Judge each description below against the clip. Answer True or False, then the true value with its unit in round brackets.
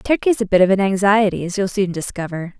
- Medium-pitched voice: False (195 Hz)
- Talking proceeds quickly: True (230 wpm)